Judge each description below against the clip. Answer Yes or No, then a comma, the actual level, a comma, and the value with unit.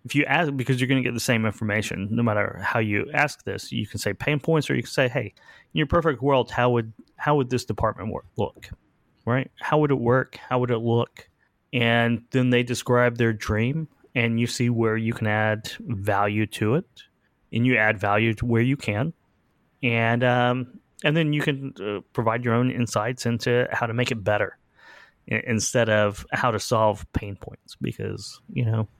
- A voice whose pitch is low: Yes, low, 120 Hz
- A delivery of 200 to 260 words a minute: Yes, fast, 205 wpm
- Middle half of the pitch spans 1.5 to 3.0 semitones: Yes, average, 2.7 semitones